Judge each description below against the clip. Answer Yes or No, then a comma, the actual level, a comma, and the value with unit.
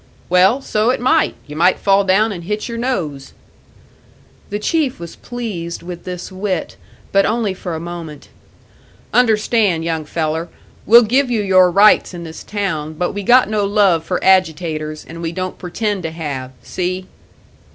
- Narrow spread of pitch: No, average, 4.1 semitones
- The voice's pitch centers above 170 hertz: Yes, medium, 185 Hz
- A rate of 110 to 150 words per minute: No, average, 165 wpm